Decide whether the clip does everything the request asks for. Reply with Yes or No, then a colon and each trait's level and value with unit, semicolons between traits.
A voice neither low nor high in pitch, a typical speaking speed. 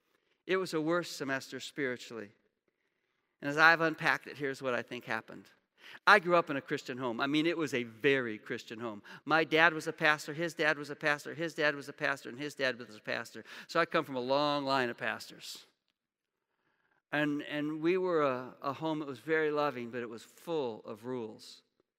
No: medium, 145 Hz; fast, 215 wpm